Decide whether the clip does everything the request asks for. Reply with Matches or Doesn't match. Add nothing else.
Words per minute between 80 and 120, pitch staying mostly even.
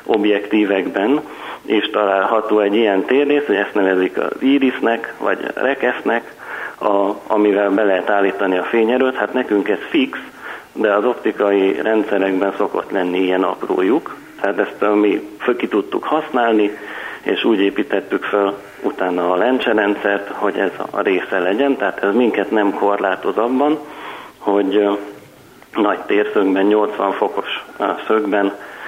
Doesn't match